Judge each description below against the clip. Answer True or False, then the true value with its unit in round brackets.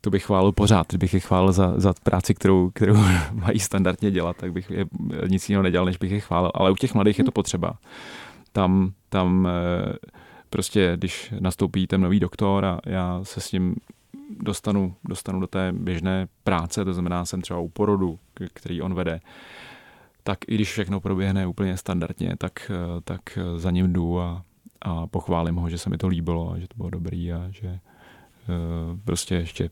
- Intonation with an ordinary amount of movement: False (1.9 semitones)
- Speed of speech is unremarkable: False (180 wpm)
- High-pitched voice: False (95 Hz)